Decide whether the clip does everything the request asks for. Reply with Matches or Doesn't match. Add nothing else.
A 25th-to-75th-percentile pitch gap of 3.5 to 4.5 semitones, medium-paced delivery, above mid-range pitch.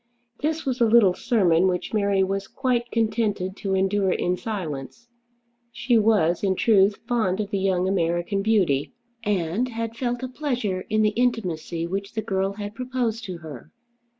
Matches